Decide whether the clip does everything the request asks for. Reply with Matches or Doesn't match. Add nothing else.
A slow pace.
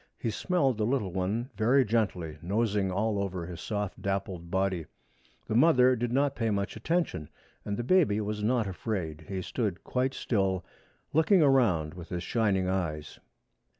Doesn't match